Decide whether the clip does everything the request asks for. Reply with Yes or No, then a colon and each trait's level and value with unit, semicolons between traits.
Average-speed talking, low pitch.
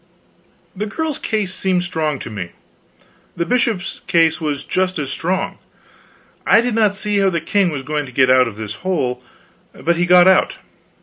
No: average, 180 wpm; medium, 175 Hz